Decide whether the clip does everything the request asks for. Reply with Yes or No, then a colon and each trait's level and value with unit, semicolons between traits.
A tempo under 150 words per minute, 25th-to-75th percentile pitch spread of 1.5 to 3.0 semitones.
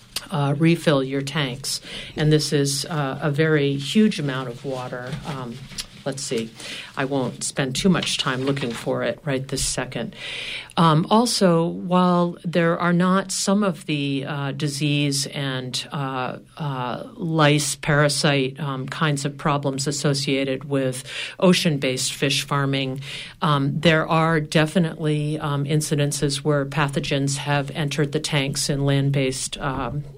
Yes: average, 140 wpm; narrow, 2.5 semitones